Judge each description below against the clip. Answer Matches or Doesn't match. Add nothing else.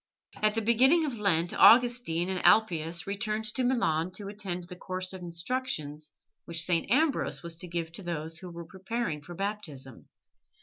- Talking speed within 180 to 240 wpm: Doesn't match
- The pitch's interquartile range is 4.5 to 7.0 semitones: Matches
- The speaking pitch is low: Doesn't match